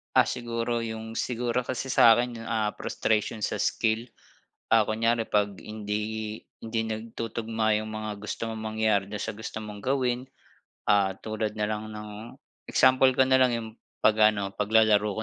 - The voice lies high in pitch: No, low, 110 Hz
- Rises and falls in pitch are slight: Yes, narrow, 1.4 semitones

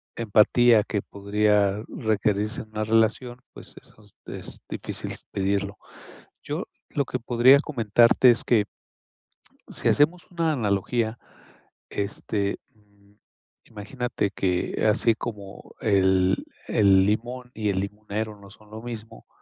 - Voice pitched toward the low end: Yes, low, 105 Hz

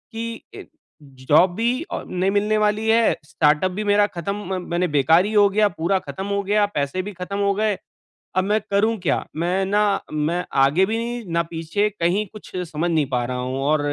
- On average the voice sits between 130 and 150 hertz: No, high, 190 Hz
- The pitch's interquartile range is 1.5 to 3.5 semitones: No, average, 3.9 semitones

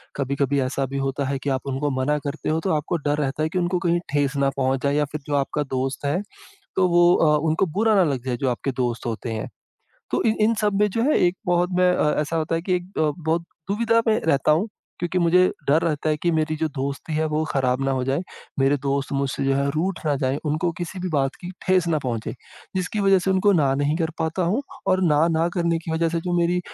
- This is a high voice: No, medium, 155 Hz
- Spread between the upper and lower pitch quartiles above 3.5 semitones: Yes, average, 4.2 semitones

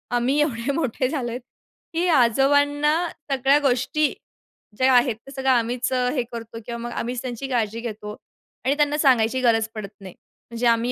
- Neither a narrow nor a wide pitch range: Yes, average, 3.1 semitones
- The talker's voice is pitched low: No, very high, 250 Hz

